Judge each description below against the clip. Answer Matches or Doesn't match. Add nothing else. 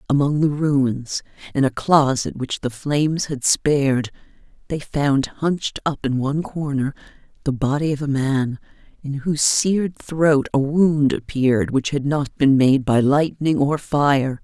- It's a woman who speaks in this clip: Matches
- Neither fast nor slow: Matches